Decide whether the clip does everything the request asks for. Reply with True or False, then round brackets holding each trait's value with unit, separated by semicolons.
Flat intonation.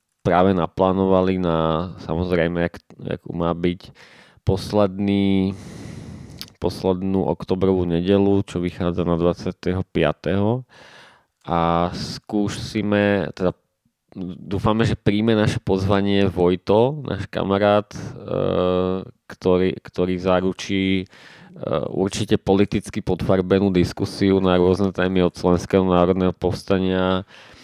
True (1.9 semitones)